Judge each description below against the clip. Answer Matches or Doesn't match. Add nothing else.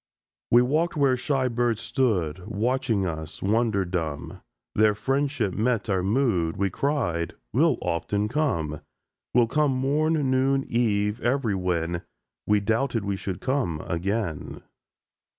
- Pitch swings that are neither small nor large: Doesn't match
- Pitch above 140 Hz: Doesn't match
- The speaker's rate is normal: Doesn't match